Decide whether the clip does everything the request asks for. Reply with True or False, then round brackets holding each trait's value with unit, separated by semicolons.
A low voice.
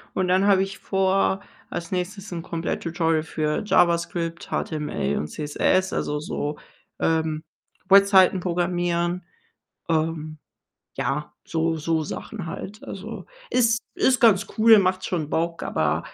False (175 Hz)